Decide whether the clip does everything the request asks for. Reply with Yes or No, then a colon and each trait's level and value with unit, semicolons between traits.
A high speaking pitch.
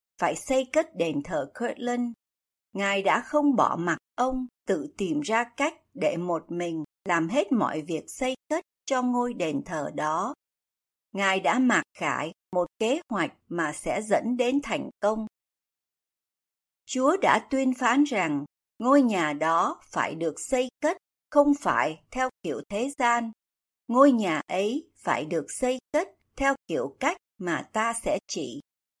Yes: high, 245 Hz